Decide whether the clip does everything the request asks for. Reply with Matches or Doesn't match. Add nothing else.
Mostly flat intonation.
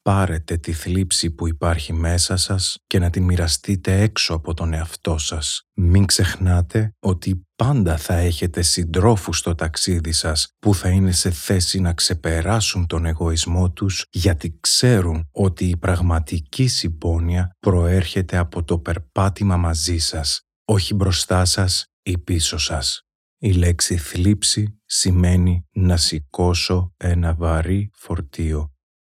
Matches